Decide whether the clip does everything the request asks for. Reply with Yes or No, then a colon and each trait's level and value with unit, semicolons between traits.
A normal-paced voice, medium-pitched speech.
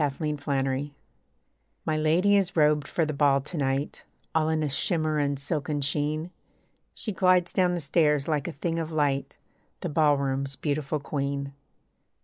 Yes: average, 155 wpm; medium, 150 Hz